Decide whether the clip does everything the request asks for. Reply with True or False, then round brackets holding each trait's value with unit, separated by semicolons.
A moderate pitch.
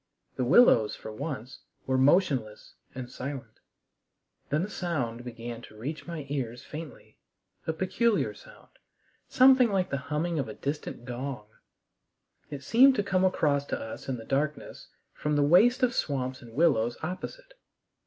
True (145 Hz)